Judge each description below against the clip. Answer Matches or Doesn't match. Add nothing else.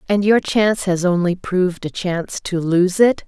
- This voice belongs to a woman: Matches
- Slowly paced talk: Doesn't match